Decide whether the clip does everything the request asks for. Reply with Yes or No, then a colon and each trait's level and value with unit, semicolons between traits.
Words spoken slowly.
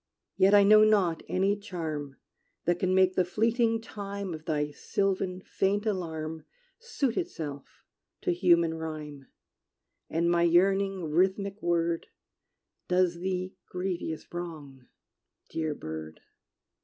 Yes: slow, 120 wpm